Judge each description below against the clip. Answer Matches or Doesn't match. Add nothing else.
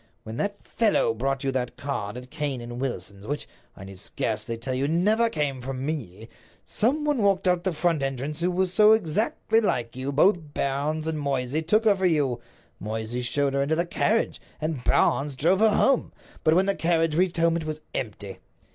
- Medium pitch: Matches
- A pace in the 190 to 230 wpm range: Matches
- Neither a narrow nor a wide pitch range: Doesn't match